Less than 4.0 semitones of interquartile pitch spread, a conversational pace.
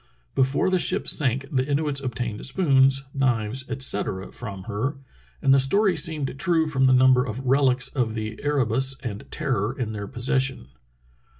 Yes: average, 2.8 semitones; average, 165 wpm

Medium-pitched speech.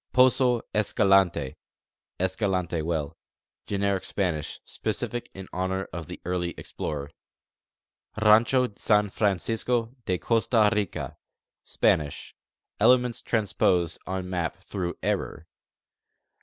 No: very low, 95 Hz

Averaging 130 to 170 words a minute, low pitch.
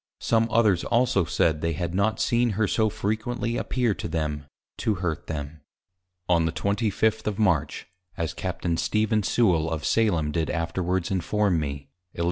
Yes: average, 160 wpm; very low, 95 Hz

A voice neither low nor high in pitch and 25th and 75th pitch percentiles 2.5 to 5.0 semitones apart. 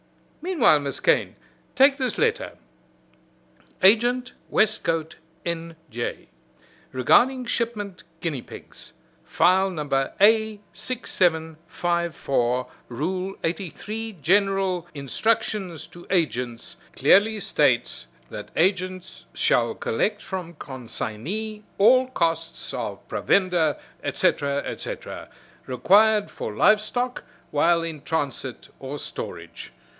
No: medium, 180 Hz; wide, 5.6 semitones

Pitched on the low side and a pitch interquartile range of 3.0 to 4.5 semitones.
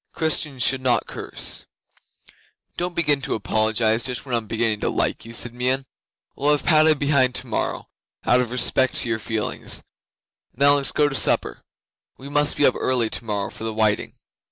Yes: low, 125 Hz; average, 4.0 semitones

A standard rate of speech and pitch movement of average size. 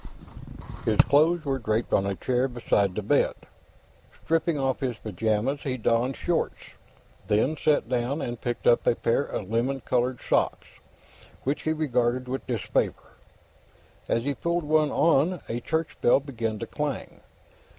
Yes: average, 150 wpm; average, 3.9 semitones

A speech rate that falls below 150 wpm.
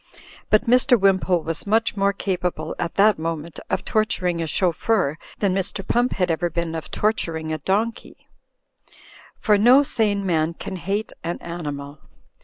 No: average, 155 wpm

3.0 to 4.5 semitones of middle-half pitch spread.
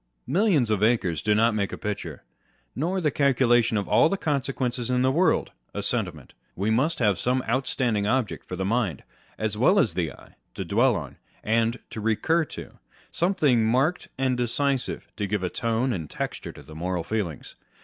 Yes: average, 4.2 semitones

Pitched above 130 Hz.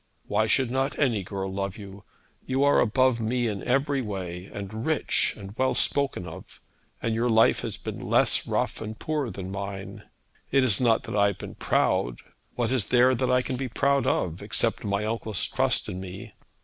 No: low, 110 Hz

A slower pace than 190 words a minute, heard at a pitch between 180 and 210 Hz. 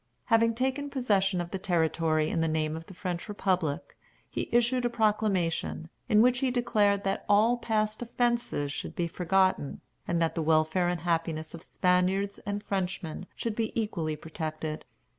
Yes: average, 165 wpm; high, 190 Hz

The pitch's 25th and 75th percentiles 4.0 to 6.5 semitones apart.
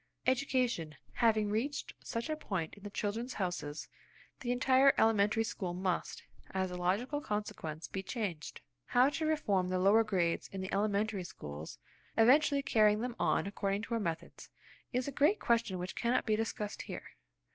Yes: average, 4.7 semitones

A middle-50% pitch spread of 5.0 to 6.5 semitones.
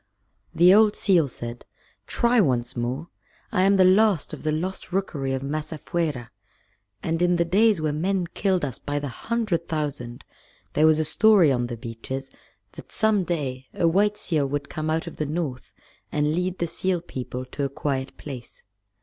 Yes: average, 5.3 semitones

